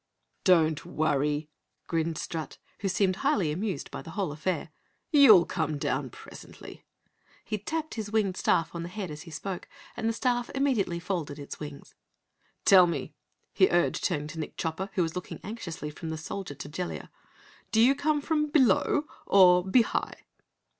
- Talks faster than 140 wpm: Yes, average, 170 wpm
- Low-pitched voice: No, medium, 180 Hz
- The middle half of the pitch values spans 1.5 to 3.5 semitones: No, wide, 5.6 semitones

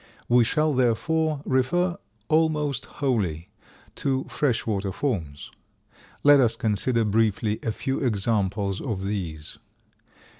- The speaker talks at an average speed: No, slow, 110 wpm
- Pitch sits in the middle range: No, low, 115 Hz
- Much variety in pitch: Yes, wide, 5.8 semitones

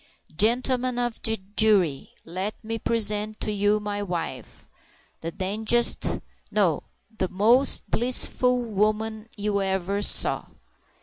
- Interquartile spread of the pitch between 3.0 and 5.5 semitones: No, narrow, 2.4 semitones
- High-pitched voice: Yes, high, 215 Hz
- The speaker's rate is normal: No, slow, 115 wpm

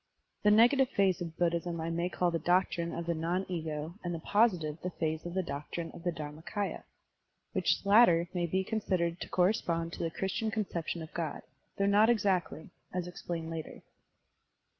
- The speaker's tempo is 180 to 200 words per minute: No, average, 165 wpm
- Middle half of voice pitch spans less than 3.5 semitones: Yes, narrow, 2.5 semitones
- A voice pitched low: No, medium, 175 Hz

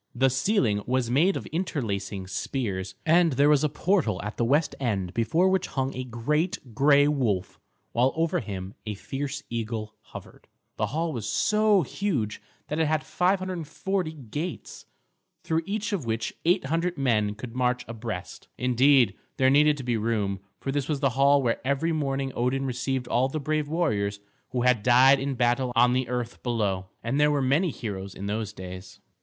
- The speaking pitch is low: Yes, low, 130 Hz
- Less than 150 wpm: No, average, 175 wpm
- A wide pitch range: No, average, 4.9 semitones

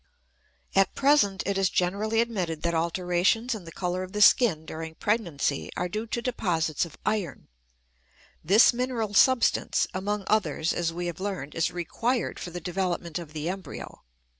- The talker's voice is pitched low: No, medium, 185 Hz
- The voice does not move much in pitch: No, average, 4.2 semitones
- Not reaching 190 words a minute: Yes, average, 165 wpm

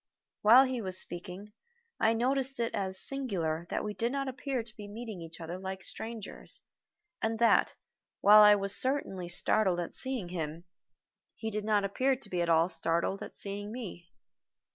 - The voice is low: No, high, 205 Hz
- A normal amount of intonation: Yes, average, 4.6 semitones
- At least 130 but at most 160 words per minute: No, average, 175 wpm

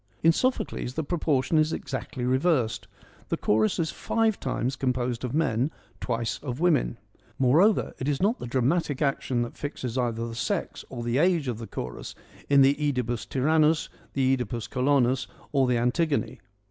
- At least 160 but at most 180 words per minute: Yes, average, 165 wpm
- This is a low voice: Yes, low, 130 Hz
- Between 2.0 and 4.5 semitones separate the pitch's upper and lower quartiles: Yes, average, 4.1 semitones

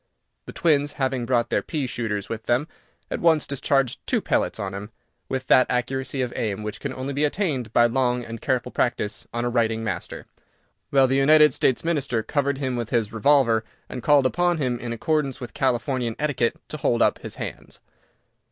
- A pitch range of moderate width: Yes, average, 3.2 semitones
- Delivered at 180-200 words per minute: Yes, average, 190 wpm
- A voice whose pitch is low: Yes, low, 130 Hz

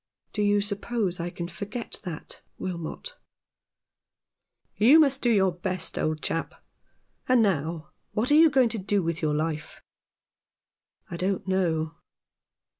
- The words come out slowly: No, average, 155 wpm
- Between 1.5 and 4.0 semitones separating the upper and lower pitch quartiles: No, average, 5.1 semitones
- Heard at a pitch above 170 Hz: Yes, high, 190 Hz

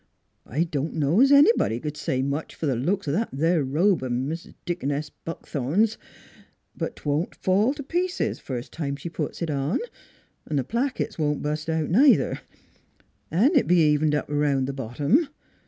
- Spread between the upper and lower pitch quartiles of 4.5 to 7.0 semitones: Yes, wide, 5.6 semitones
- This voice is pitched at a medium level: Yes, medium, 155 Hz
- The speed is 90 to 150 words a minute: No, average, 180 wpm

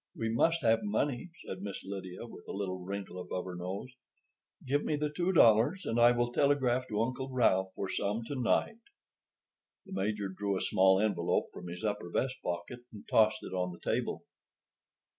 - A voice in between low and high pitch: No, low, 110 Hz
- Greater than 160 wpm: Yes, average, 185 wpm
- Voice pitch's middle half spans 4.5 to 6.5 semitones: Yes, average, 4.8 semitones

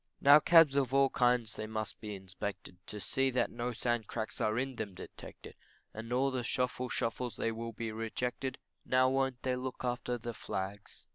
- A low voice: Yes, low, 120 Hz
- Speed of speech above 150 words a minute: Yes, average, 190 wpm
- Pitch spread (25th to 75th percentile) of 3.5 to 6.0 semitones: No, average, 2.8 semitones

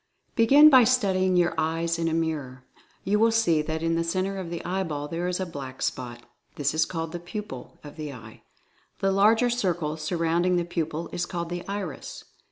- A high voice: No, medium, 170 Hz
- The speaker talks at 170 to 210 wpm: Yes, average, 195 wpm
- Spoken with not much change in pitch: No, average, 3.3 semitones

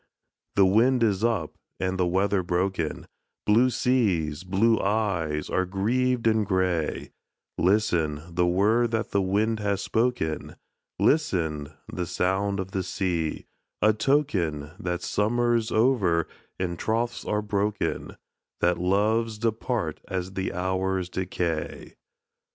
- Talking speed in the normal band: No, slow, 120 wpm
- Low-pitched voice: Yes, very low, 95 Hz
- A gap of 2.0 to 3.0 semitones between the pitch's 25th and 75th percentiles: No, average, 4.0 semitones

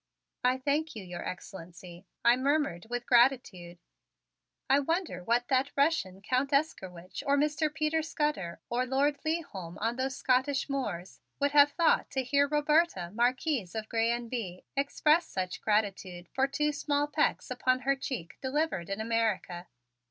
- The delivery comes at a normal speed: Yes, average, 150 wpm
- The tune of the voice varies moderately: No, wide, 6.6 semitones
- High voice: Yes, very high, 255 Hz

